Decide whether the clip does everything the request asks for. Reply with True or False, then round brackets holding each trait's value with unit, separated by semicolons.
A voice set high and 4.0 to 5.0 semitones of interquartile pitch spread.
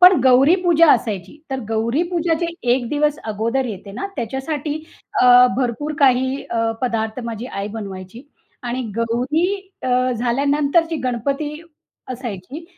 True (255 Hz; 4.5 semitones)